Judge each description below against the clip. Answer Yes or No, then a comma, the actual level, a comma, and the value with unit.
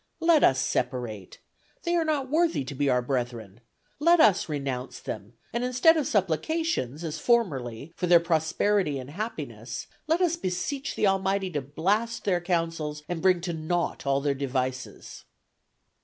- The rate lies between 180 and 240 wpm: No, average, 155 wpm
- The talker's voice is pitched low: No, medium, 170 Hz